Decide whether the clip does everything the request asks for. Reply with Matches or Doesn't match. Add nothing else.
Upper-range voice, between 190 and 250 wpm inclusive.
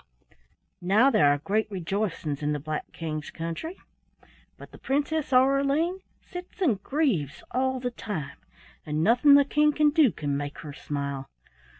Doesn't match